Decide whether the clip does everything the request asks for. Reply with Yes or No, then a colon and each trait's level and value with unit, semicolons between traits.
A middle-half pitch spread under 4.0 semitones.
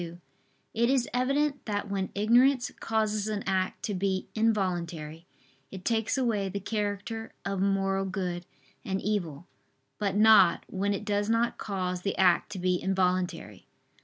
Yes: average, 2.9 semitones